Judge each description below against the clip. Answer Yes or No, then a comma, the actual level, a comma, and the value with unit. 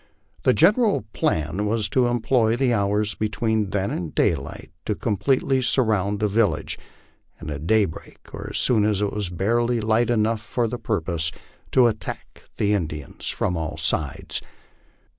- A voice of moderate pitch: No, low, 105 Hz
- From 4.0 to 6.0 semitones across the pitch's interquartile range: No, average, 3.4 semitones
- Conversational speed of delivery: Yes, average, 160 wpm